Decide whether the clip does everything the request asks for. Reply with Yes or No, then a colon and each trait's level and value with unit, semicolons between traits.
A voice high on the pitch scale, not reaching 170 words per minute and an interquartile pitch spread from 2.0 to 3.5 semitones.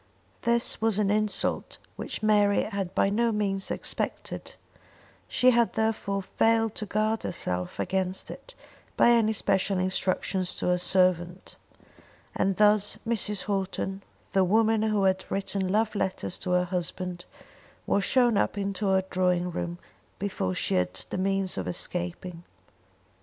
Yes: high, 195 Hz; average, 140 wpm; average, 2.7 semitones